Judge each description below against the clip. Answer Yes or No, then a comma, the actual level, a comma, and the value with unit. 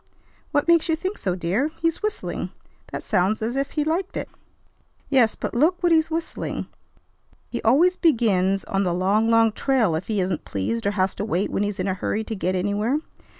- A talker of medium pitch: No, high, 220 Hz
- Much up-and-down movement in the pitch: Yes, wide, 8.3 semitones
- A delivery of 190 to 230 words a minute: Yes, average, 200 wpm